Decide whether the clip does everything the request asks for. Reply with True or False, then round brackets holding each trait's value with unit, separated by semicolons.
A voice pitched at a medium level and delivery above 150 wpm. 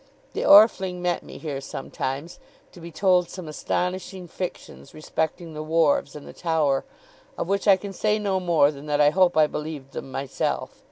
True (165 Hz; 180 wpm)